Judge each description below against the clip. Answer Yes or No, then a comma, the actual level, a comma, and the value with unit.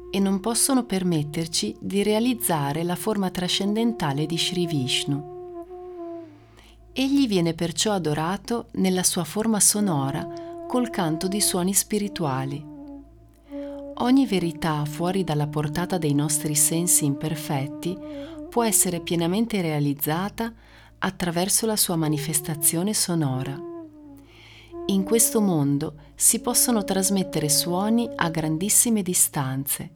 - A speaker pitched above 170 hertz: Yes, medium, 185 Hz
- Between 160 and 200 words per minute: No, slow, 105 wpm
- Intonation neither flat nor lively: No, wide, 6.4 semitones